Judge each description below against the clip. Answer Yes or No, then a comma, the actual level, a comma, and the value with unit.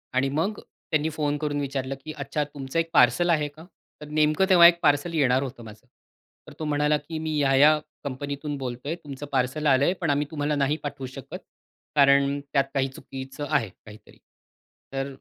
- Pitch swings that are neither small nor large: No, narrow, 2.1 semitones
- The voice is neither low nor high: Yes, medium, 145 Hz